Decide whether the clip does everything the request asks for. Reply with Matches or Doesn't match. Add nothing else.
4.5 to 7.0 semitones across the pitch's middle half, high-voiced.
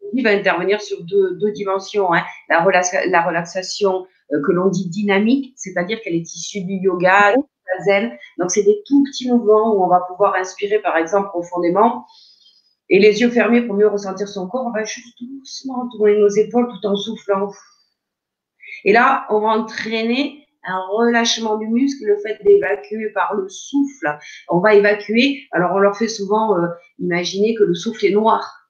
Doesn't match